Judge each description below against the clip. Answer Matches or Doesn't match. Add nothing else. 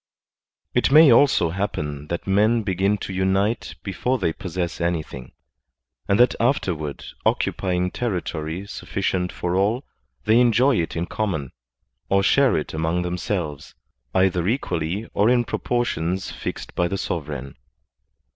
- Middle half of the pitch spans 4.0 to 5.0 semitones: Matches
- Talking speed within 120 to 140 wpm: Matches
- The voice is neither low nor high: Doesn't match